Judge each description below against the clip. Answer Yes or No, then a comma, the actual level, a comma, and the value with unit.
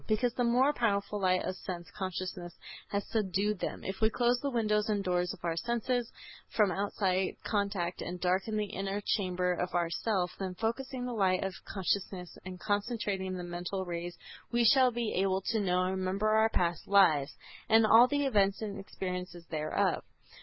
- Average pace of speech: Yes, average, 180 wpm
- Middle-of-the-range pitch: No, high, 195 Hz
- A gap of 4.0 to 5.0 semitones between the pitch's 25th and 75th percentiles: No, average, 3.3 semitones